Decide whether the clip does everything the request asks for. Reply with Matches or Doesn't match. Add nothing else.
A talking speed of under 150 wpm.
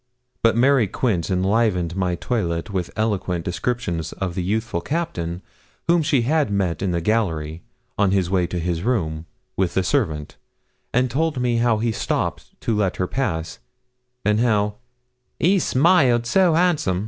Doesn't match